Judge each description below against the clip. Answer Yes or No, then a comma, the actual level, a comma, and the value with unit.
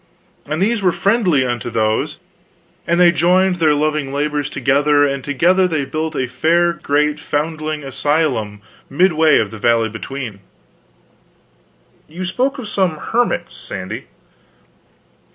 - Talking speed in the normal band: No, slow, 130 wpm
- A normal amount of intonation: Yes, average, 4.1 semitones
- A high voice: No, medium, 150 Hz